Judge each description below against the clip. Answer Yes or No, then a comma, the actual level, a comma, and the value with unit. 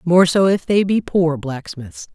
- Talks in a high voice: No, medium, 170 Hz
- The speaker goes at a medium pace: Yes, average, 195 wpm